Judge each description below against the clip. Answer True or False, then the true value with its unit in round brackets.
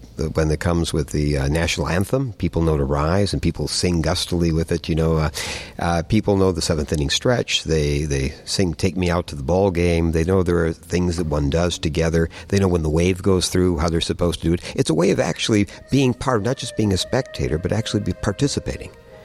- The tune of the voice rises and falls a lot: False (3.0 semitones)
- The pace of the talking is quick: True (240 wpm)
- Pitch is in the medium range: False (85 Hz)